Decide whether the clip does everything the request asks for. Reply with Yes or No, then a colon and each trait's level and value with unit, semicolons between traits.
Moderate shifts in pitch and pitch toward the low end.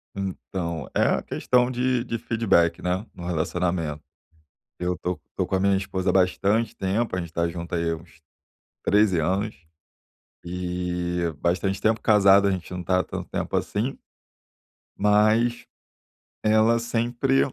Yes: average, 3.8 semitones; very low, 95 Hz